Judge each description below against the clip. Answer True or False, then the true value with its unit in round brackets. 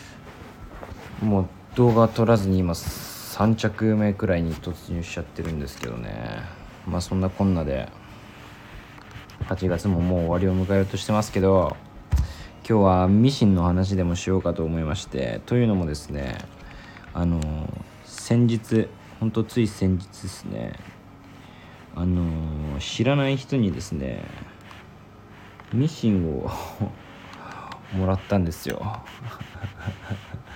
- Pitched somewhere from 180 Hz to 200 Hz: False (95 Hz)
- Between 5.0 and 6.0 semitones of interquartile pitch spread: False (3.8 semitones)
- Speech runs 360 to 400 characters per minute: False (240 characters per minute)